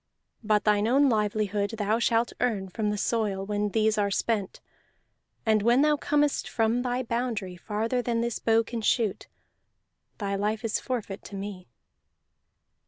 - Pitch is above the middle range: Yes, high, 220 Hz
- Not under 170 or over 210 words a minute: No, average, 155 wpm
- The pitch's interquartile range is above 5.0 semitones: No, narrow, 2.4 semitones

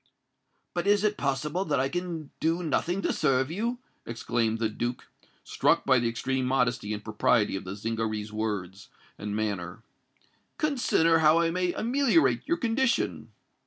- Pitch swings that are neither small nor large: No, wide, 8.1 semitones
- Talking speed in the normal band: Yes, average, 155 wpm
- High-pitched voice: No, low, 135 Hz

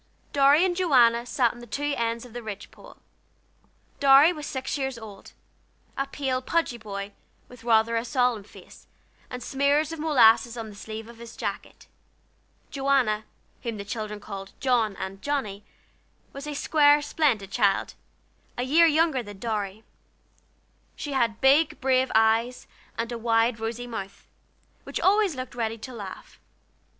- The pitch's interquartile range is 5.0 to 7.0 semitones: No, average, 4.0 semitones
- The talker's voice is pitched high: Yes, high, 240 Hz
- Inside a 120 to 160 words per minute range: Yes, average, 155 wpm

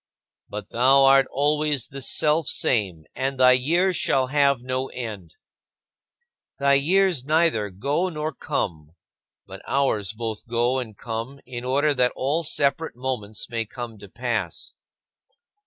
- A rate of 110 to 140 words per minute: Yes, slow, 135 wpm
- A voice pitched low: Yes, low, 130 Hz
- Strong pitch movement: No, average, 3.9 semitones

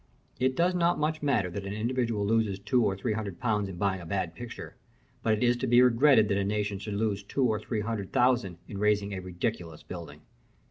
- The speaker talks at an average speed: No, fast, 225 wpm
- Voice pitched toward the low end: Yes, low, 105 Hz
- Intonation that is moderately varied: Yes, average, 3.8 semitones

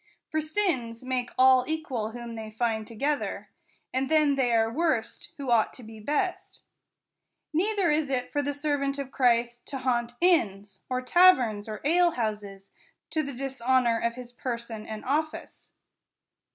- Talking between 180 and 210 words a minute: No, average, 150 wpm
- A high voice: Yes, very high, 255 Hz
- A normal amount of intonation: Yes, average, 4.2 semitones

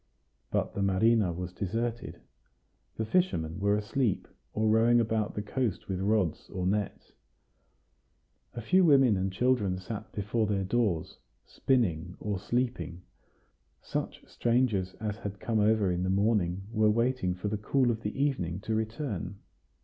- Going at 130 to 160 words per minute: Yes, average, 150 wpm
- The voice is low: Yes, low, 105 Hz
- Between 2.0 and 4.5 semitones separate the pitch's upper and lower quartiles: Yes, average, 3.8 semitones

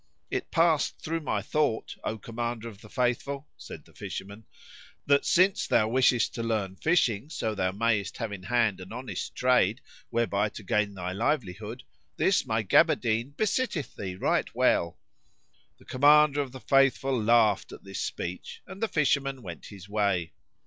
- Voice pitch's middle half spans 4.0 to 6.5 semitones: Yes, average, 5.2 semitones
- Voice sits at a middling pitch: No, low, 115 Hz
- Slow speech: No, average, 165 wpm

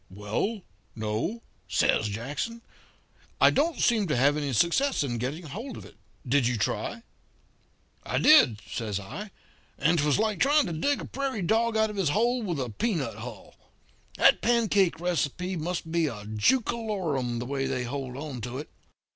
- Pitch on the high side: No, medium, 160 Hz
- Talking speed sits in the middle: Yes, average, 170 wpm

